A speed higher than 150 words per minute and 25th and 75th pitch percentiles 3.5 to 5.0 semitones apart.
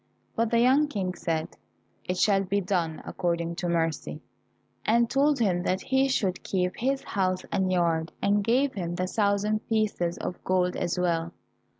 Yes: average, 170 wpm; average, 4.0 semitones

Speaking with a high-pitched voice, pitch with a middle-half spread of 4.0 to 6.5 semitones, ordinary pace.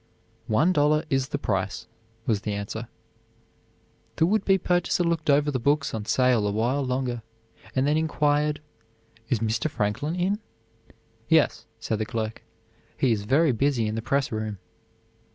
No: low, 130 Hz; average, 5.3 semitones; average, 155 wpm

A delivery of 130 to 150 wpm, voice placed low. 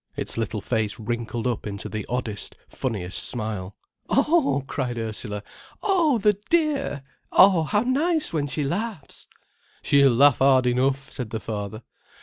Yes: average, 140 wpm; low, 130 Hz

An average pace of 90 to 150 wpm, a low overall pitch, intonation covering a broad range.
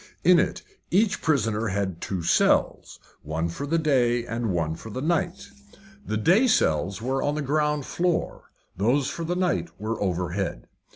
No: average, 165 wpm; low, 120 Hz; wide, 8.8 semitones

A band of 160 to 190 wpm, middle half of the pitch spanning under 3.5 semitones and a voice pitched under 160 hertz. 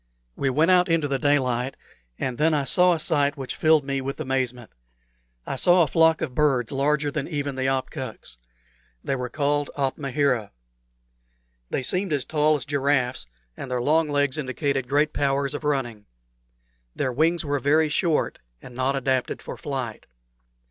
Yes: average, 165 wpm; narrow, 2.5 semitones; medium, 140 Hz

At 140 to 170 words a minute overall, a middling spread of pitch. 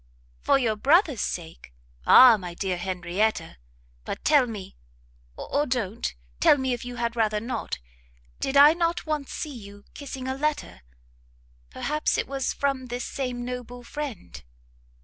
Yes: average, 150 wpm; average, 5.0 semitones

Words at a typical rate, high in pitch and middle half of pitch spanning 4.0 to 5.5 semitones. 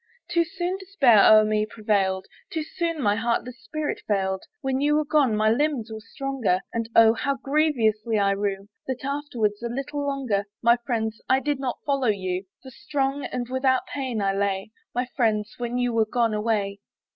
Yes: average, 180 wpm; high, 235 Hz; average, 4.4 semitones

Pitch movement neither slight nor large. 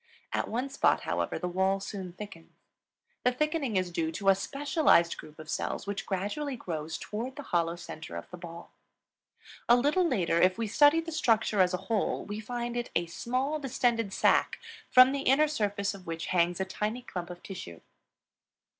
No: wide, 6.2 semitones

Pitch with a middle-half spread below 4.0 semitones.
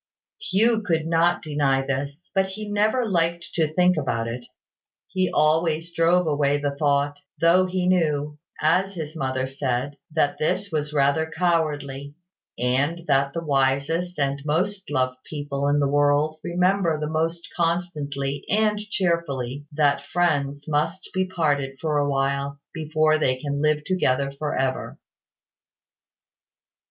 Yes: average, 3.4 semitones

